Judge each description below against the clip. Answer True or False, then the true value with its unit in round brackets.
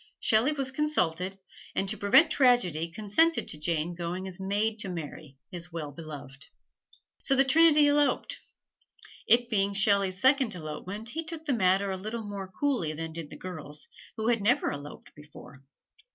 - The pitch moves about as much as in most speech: False (6.8 semitones)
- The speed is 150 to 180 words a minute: True (165 wpm)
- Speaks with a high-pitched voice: True (195 Hz)